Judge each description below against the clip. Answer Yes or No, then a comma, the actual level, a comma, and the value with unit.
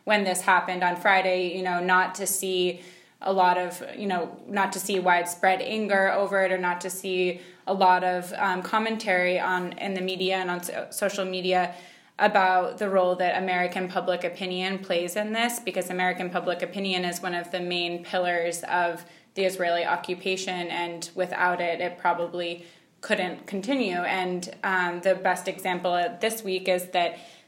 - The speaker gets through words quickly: No, average, 175 wpm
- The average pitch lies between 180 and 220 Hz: Yes, medium, 185 Hz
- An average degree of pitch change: No, narrow, 1.2 semitones